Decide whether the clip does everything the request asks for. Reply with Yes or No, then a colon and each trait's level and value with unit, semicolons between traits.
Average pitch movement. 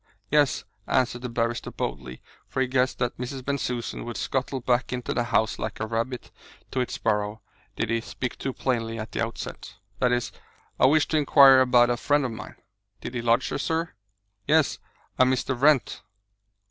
No: narrow, 2.2 semitones